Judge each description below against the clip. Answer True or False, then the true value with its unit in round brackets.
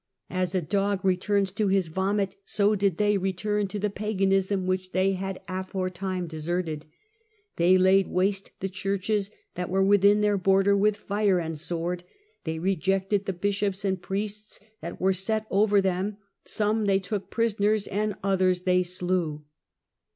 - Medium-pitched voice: False (195 Hz)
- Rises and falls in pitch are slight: True (1.8 semitones)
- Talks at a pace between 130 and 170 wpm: True (160 wpm)